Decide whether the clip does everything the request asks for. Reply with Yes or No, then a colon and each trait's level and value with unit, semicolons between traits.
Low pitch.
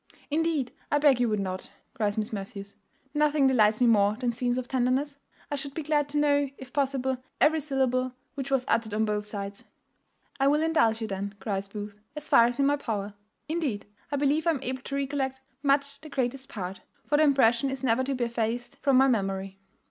No: very high, 255 Hz